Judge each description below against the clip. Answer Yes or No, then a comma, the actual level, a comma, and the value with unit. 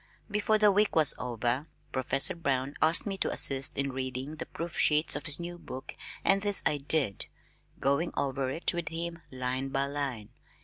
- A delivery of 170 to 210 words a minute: Yes, average, 180 wpm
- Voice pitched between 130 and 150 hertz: Yes, medium, 140 Hz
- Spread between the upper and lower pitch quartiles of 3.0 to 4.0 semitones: No, average, 4.4 semitones